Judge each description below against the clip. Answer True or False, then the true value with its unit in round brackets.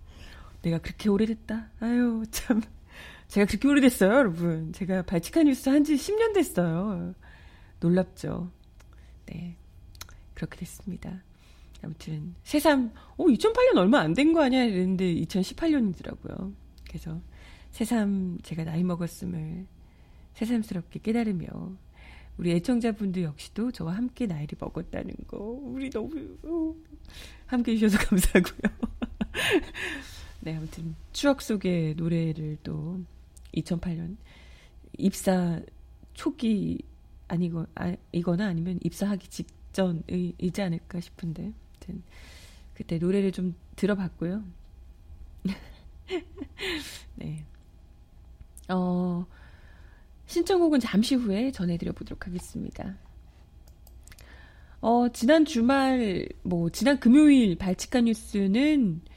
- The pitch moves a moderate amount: False (5.7 semitones)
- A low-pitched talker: False (190 Hz)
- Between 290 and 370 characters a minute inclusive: False (230 characters per minute)